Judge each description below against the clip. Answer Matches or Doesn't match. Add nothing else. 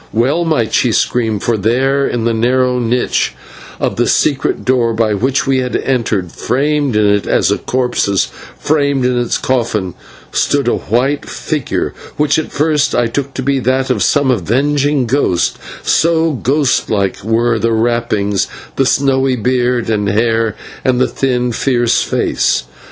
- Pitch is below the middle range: Matches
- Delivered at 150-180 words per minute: Matches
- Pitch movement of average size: Matches